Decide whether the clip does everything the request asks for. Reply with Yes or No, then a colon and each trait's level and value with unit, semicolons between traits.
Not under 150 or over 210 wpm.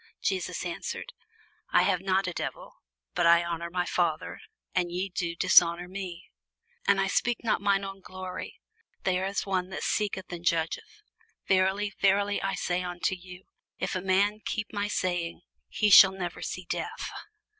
Yes: average, 165 wpm